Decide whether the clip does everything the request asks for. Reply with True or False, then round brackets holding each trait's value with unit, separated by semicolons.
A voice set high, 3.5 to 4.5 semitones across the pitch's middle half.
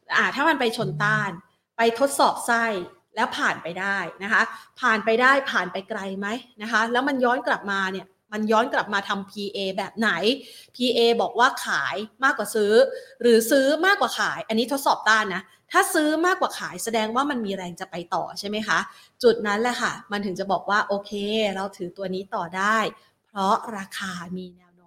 True (220 Hz; 4.1 semitones)